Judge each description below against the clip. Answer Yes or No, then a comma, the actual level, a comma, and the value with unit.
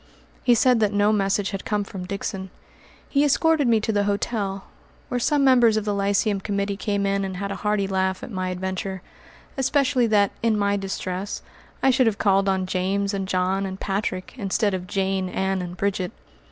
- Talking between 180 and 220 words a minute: Yes, average, 195 wpm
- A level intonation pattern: Yes, narrow, 2.1 semitones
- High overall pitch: Yes, high, 200 Hz